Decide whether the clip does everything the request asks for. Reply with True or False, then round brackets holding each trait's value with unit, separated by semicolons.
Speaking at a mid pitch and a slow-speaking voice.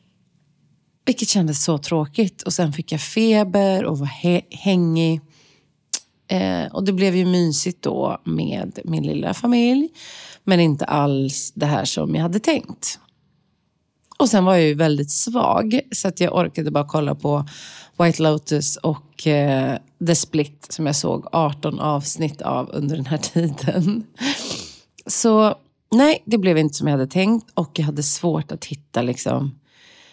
False (160 Hz; 155 wpm)